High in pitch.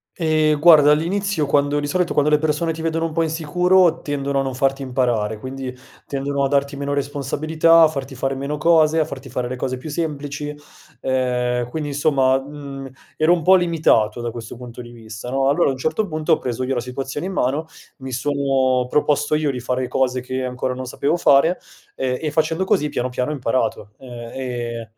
No: medium, 140 Hz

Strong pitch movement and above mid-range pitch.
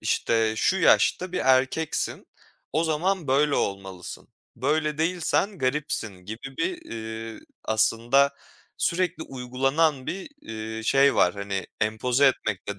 No: wide, 6.1 semitones; low, 135 Hz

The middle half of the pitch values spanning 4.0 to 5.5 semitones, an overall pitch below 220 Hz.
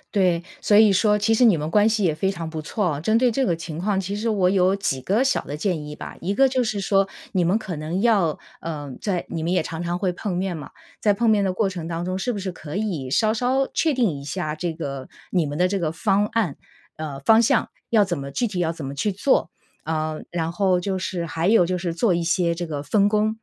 Yes: average, 4.3 semitones; medium, 185 Hz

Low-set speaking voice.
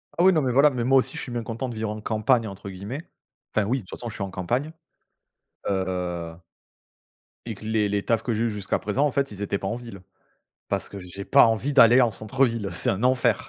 Yes: low, 115 Hz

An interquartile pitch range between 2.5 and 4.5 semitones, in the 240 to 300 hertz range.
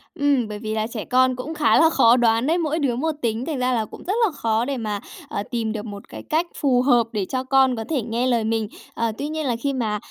Yes: average, 3.9 semitones; high, 245 Hz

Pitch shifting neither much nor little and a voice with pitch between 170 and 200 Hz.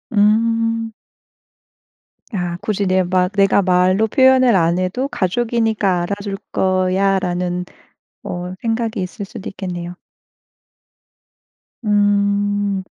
Yes: average, 3.0 semitones; high, 195 Hz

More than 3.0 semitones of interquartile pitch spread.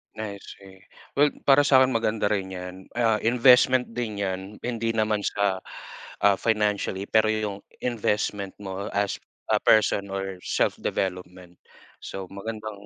No: average, 2.7 semitones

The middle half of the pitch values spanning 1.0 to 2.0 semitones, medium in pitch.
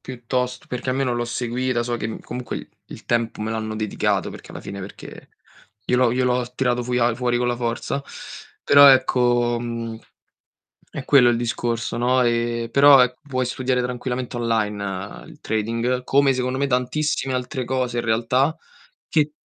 No: narrow, 1.5 semitones; low, 125 Hz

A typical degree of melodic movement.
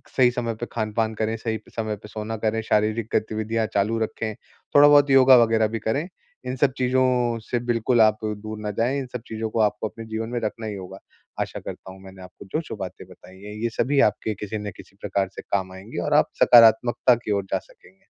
No: narrow, 2.2 semitones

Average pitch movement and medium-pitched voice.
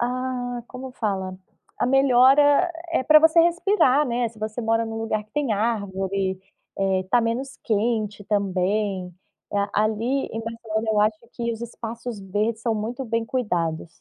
No: average, 3.2 semitones; high, 225 Hz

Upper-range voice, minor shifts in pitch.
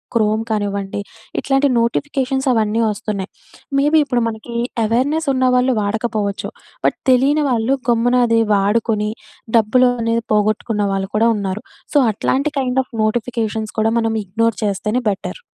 No: high, 230 Hz; average, 3.1 semitones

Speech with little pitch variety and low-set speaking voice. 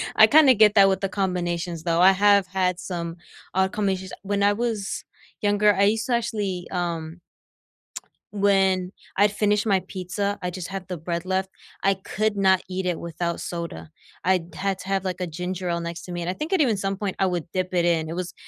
No: narrow, 2.3 semitones; high, 190 Hz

